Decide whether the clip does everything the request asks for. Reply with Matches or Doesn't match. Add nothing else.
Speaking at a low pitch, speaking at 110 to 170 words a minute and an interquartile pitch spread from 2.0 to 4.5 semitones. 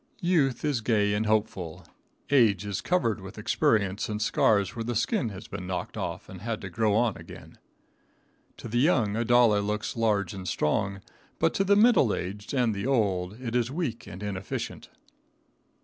Doesn't match